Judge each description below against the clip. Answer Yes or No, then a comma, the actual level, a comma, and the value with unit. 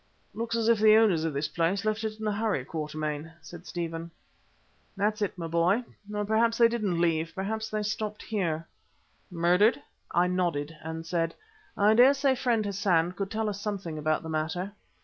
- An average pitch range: Yes, average, 4.7 semitones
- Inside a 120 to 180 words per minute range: No, average, 190 wpm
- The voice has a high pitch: Yes, high, 195 Hz